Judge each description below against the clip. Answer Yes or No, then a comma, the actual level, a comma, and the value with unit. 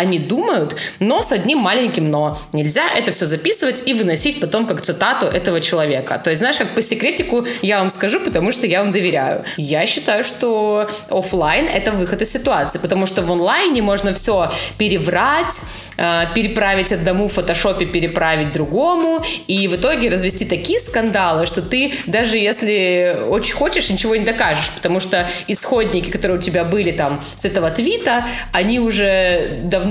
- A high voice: Yes, high, 195 Hz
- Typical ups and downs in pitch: Yes, average, 4.2 semitones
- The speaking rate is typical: No, fast, 165 wpm